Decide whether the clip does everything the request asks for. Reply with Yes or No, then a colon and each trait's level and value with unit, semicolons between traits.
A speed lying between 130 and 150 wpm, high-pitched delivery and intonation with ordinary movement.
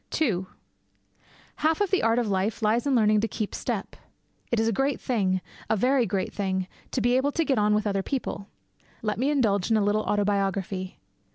No: average, 195 wpm; high, 215 Hz; average, 3.9 semitones